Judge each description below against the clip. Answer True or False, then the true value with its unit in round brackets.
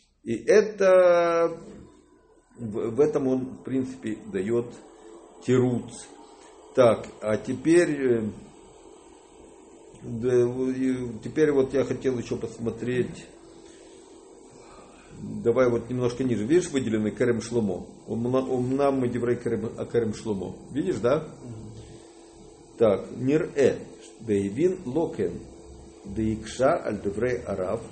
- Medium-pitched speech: False (125 Hz)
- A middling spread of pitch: False (6.8 semitones)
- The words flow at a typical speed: False (90 wpm)